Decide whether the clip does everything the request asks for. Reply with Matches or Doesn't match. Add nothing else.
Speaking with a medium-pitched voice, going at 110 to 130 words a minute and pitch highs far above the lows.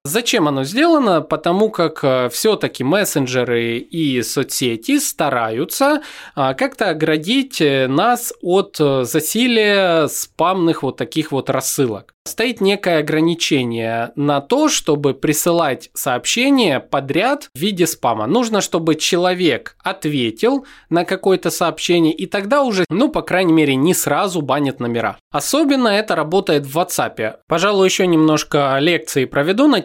Matches